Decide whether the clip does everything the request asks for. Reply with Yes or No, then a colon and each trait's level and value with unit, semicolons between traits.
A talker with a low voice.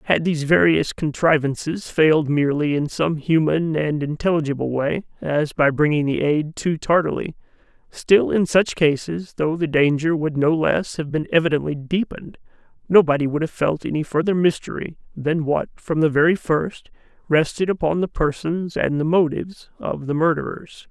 No: medium, 155 Hz